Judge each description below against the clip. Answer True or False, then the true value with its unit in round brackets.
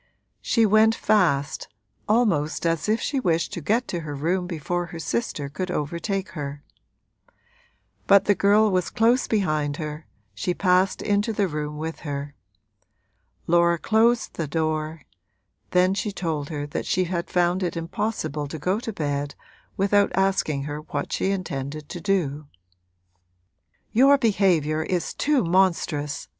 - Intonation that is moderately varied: True (4.8 semitones)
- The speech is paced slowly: False (145 wpm)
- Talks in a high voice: False (175 Hz)